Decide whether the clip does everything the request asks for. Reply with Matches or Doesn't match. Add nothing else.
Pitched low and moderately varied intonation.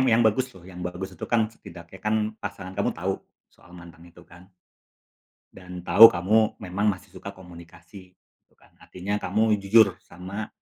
Matches